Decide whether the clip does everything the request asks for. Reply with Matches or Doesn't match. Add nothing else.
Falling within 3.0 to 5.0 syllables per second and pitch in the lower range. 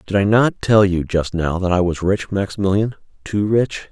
Matches